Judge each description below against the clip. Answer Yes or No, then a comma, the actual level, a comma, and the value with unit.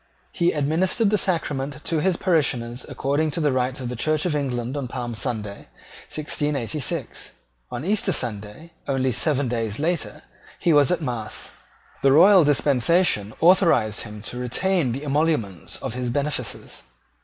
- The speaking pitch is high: No, medium, 140 Hz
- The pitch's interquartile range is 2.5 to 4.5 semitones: No, average, 4.9 semitones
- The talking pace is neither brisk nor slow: Yes, average, 150 wpm